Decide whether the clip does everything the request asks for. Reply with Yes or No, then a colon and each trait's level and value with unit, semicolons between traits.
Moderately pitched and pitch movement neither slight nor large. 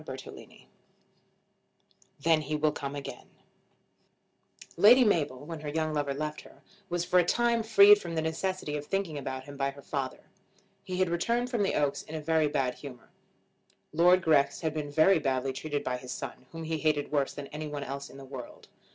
Yes: medium, 155 Hz; average, 3.5 semitones